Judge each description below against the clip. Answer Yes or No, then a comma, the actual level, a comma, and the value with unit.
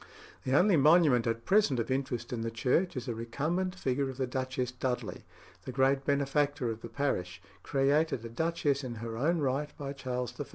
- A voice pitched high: No, low, 135 Hz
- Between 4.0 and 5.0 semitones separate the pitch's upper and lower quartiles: No, average, 3.1 semitones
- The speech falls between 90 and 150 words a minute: No, average, 195 wpm